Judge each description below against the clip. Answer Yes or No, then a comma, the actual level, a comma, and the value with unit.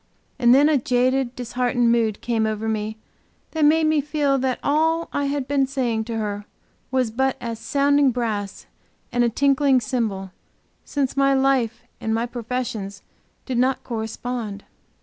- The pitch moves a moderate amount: Yes, average, 3.5 semitones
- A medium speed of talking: Yes, average, 155 wpm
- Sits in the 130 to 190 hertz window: No, very high, 250 Hz